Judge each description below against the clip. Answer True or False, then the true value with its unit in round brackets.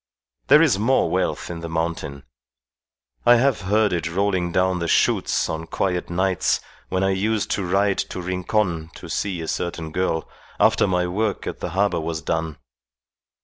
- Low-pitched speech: True (90 Hz)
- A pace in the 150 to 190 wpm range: True (170 wpm)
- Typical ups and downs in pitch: True (3.3 semitones)